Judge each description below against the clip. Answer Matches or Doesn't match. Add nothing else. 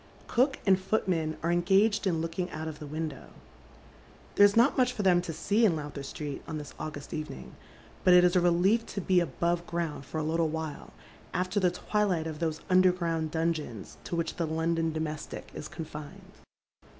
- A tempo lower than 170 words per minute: Doesn't match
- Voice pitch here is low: Doesn't match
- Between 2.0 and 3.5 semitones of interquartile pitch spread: Matches